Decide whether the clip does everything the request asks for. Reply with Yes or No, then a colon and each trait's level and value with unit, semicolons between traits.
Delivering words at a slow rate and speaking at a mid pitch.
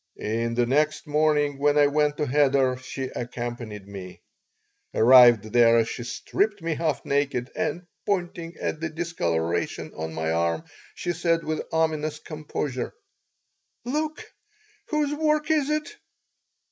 Yes: slow, 130 wpm; medium, 145 Hz